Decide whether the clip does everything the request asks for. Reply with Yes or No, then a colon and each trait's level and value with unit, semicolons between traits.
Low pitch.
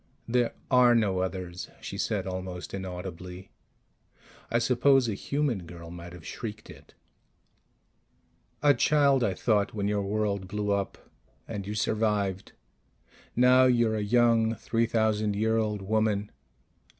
Yes: low, 105 Hz